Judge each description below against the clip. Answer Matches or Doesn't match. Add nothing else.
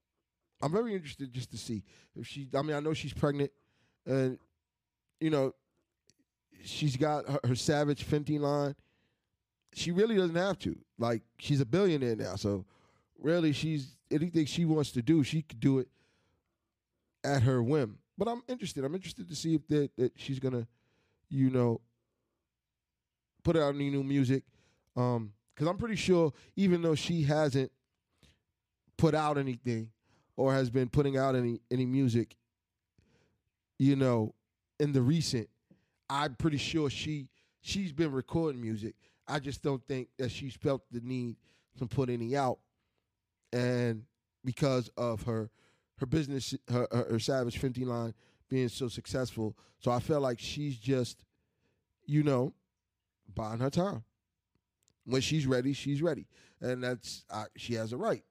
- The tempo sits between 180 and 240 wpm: Doesn't match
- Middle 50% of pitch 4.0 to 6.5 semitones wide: Matches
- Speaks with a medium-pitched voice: Doesn't match